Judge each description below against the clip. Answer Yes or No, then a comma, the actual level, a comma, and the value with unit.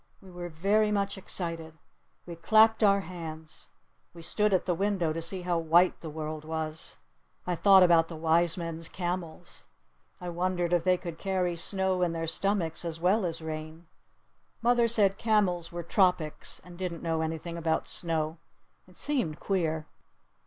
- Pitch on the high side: No, medium, 175 Hz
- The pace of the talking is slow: No, average, 165 wpm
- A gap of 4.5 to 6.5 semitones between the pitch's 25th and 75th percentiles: No, average, 2.7 semitones